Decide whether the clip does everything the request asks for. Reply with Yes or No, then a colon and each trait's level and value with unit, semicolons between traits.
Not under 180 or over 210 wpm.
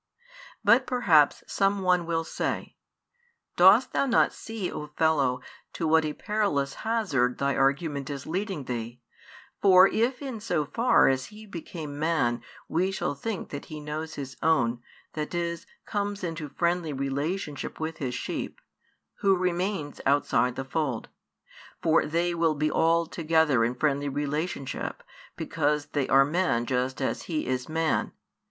No: average, 150 wpm